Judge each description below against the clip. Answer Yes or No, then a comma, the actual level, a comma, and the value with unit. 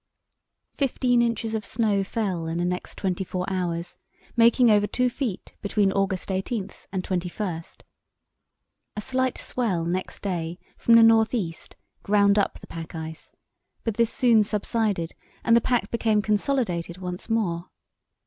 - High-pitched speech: Yes, high, 205 Hz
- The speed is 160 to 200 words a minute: No, average, 150 wpm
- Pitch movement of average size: Yes, average, 4.2 semitones